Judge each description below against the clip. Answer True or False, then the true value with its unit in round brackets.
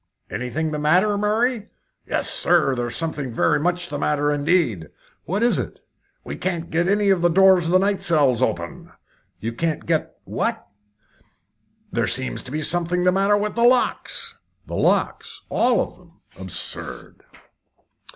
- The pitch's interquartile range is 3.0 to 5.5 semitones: True (5.0 semitones)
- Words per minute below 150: False (160 wpm)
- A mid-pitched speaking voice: True (170 Hz)